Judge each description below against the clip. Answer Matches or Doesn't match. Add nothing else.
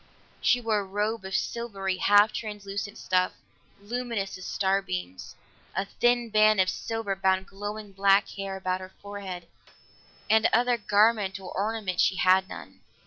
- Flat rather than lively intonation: Matches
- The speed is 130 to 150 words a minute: Matches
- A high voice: Matches